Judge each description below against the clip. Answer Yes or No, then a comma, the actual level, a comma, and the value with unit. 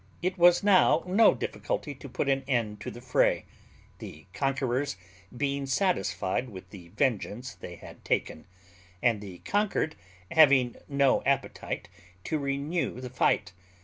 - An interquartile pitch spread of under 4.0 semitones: No, average, 4.9 semitones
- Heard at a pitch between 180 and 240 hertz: No, low, 135 Hz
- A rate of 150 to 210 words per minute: No, average, 140 wpm